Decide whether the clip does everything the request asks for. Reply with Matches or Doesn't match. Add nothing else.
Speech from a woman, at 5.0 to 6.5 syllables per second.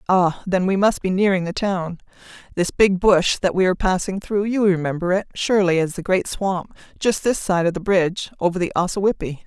Matches